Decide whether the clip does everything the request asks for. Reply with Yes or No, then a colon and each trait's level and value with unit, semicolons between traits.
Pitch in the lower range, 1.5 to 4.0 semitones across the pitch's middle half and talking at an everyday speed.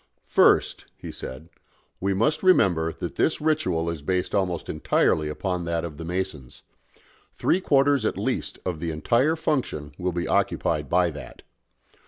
No: very low, 90 Hz; average, 5.3 semitones; average, 155 wpm